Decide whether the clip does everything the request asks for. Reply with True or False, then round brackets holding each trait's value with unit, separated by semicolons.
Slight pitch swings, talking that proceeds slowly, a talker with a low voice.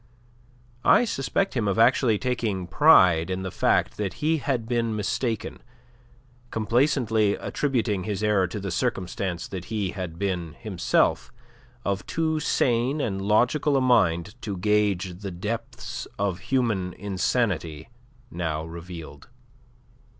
False (4.7 semitones; 130 wpm; 105 Hz)